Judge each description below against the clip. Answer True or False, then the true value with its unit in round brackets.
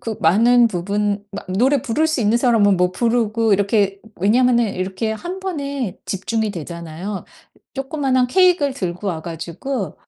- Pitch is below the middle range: False (220 Hz)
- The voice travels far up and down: False (4.9 semitones)